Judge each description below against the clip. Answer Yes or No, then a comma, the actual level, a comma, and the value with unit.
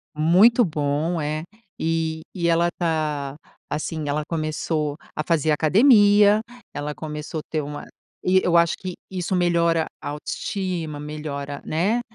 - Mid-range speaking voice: Yes, medium, 160 Hz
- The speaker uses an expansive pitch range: No, average, 2.8 semitones